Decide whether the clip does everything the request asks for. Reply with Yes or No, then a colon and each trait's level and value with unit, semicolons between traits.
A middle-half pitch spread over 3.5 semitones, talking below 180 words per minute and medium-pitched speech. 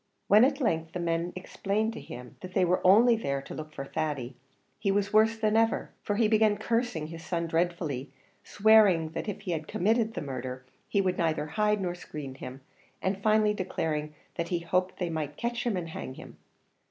No: average, 5.3 semitones; average, 200 wpm; medium, 180 Hz